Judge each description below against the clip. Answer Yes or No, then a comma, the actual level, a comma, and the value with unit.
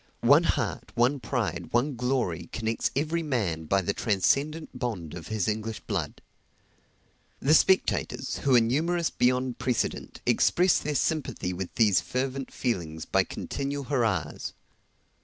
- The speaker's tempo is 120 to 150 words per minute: Yes, slow, 135 wpm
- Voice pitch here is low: Yes, low, 120 Hz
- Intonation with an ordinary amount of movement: No, wide, 6.2 semitones